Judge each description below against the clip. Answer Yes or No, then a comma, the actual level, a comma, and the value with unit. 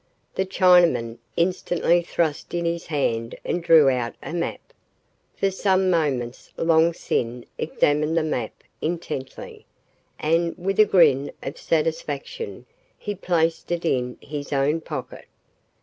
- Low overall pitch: No, medium, 165 Hz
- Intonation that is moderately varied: Yes, average, 3.5 semitones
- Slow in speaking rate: Yes, slow, 130 wpm